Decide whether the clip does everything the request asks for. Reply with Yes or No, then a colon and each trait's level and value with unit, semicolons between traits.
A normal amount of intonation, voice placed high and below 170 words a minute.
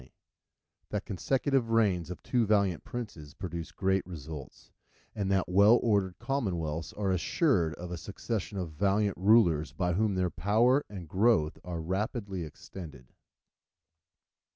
No: average, 4.2 semitones; very low, 95 Hz; slow, 135 wpm